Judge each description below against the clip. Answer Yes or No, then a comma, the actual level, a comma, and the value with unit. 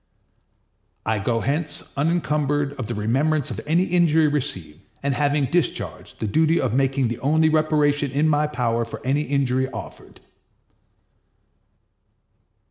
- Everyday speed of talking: No, slow, 130 wpm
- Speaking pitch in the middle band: Yes, medium, 145 Hz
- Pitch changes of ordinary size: Yes, average, 3.4 semitones